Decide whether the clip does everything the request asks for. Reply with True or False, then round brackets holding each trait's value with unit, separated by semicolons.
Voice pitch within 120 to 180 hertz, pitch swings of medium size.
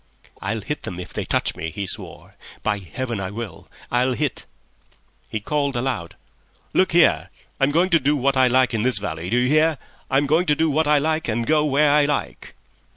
True (135 Hz; 4.8 semitones)